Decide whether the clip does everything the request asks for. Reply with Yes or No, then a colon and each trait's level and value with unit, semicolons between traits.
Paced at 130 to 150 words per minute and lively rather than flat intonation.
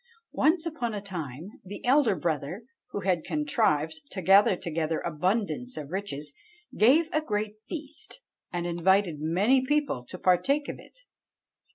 Yes: average, 145 wpm; wide, 7.4 semitones